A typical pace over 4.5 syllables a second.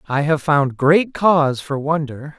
No: 4.1 syllables/s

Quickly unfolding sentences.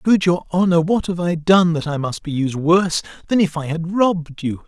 Yes: fast, 245 wpm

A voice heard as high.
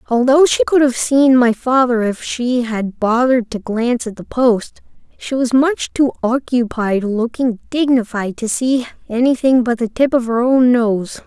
Yes: high, 245 Hz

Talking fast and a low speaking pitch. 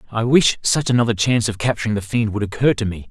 Yes: fast, 250 wpm; low, 110 Hz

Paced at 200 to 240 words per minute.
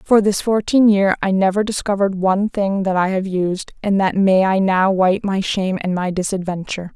Yes: fast, 205 wpm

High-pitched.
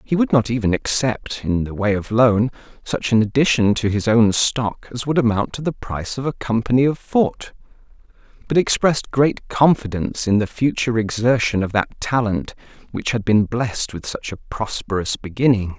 No: low, 115 Hz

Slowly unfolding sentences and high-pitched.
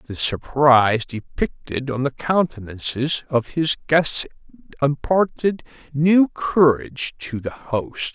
No: slow, 110 wpm; medium, 140 Hz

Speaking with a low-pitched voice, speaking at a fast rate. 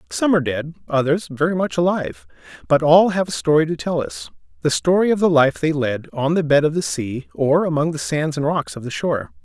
No: medium, 145 Hz; fast, 230 wpm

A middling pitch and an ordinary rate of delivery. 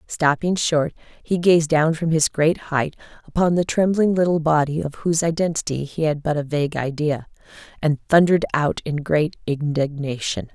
Yes: medium, 155 Hz; average, 165 wpm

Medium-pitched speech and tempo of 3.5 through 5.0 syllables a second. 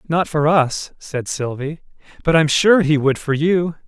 Yes: medium, 155 Hz; 4.1 syllables/s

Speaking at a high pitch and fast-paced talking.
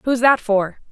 No: high, 230 Hz; average, 195 wpm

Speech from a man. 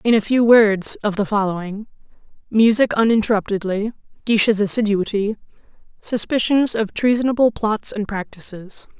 No: female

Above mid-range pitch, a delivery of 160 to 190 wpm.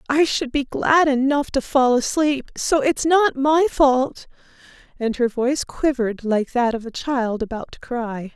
Yes: very high, 265 Hz; average, 180 wpm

